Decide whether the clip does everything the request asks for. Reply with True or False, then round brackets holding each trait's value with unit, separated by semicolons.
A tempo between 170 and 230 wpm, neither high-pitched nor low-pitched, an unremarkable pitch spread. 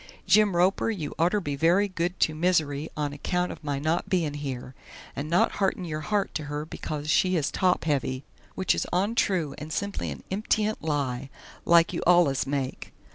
True (185 wpm; 165 Hz; 4.2 semitones)